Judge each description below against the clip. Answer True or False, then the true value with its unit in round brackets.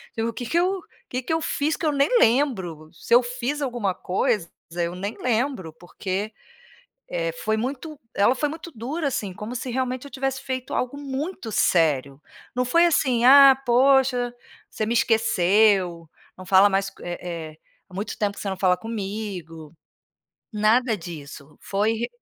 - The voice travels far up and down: True (5.9 semitones)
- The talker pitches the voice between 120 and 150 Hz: False (225 Hz)